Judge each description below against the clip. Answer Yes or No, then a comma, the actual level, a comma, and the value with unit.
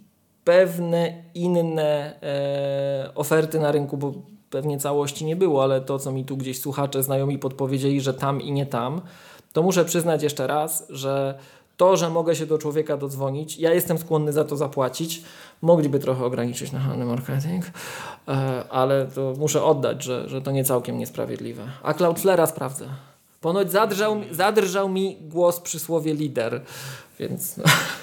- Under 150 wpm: No, average, 155 wpm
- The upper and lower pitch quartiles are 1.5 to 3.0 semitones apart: No, average, 3.7 semitones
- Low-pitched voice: No, medium, 150 Hz